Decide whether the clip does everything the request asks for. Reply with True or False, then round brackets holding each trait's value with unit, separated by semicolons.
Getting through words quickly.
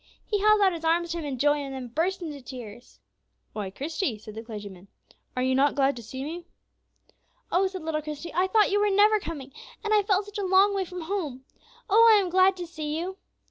True (235 wpm)